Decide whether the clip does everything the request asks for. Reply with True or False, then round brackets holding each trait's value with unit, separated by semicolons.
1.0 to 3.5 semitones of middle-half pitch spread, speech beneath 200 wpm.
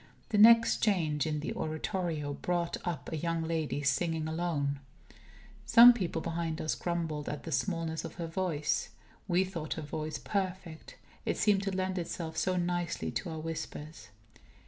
True (2.7 semitones; 160 wpm)